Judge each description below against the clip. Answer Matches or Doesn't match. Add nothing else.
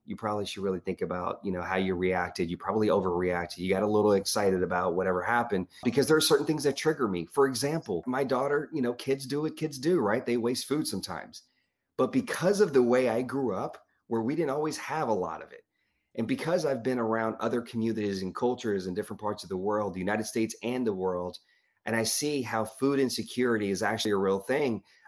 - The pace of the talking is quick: Matches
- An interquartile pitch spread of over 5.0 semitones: Matches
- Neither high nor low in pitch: Doesn't match